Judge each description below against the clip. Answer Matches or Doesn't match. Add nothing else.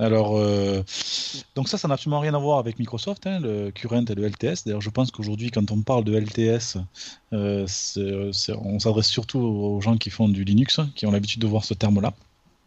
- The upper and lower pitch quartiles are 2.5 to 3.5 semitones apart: Matches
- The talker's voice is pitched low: Matches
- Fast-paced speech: Matches